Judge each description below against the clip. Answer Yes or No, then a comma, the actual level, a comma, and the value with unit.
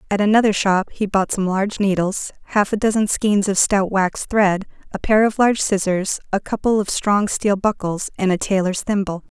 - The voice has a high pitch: Yes, high, 200 Hz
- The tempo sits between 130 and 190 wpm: No, average, 200 wpm